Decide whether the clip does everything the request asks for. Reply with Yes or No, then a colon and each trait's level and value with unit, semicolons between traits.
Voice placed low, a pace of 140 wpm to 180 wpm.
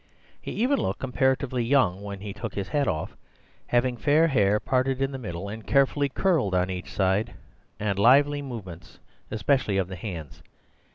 Yes: low, 115 Hz; average, 170 wpm